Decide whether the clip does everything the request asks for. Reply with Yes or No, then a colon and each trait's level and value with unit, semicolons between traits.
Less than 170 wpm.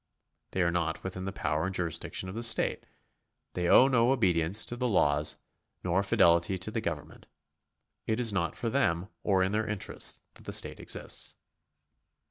No: average, 175 wpm